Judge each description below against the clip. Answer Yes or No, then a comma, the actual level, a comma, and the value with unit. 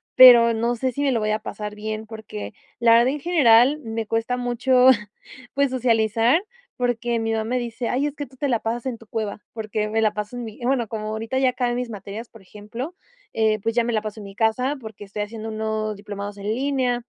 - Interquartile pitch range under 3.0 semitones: Yes, narrow, 2.5 semitones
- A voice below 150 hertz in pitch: No, high, 225 Hz